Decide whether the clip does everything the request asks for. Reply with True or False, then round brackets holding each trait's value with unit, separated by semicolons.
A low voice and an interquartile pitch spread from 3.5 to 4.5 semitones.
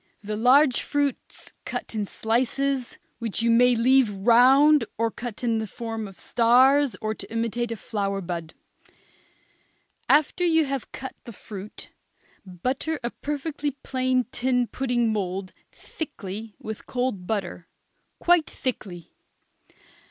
False (240 Hz; 3.9 semitones)